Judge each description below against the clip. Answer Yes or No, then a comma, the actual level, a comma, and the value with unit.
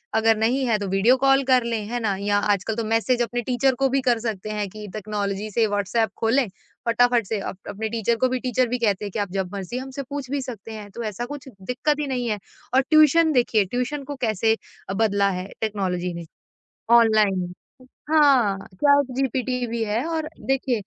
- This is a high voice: Yes, high, 230 Hz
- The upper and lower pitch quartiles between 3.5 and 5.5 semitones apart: Yes, average, 3.8 semitones